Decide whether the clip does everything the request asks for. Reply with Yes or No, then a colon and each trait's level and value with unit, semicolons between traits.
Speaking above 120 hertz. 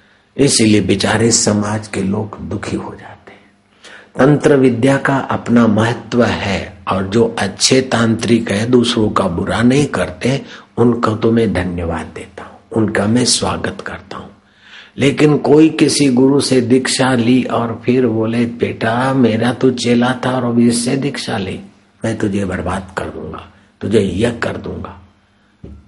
No: low, 115 Hz